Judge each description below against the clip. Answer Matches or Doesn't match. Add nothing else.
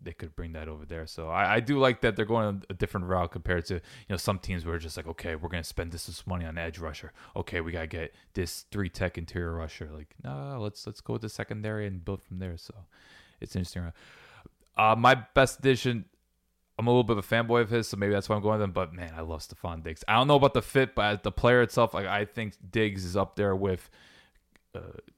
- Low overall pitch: Matches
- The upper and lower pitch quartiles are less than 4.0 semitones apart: Doesn't match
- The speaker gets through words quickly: Matches